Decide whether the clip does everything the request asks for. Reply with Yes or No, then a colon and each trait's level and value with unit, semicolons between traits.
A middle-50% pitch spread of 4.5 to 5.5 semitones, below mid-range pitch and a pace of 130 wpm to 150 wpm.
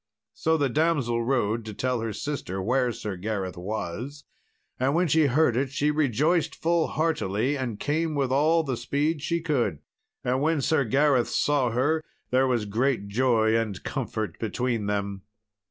No: average, 5.0 semitones; low, 130 Hz; average, 165 wpm